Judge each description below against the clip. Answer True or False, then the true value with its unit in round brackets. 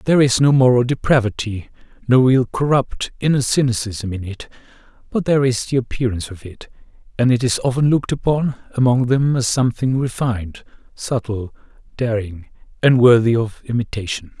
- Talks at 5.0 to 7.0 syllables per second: True (5.4 syllables/s)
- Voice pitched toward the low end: True (120 Hz)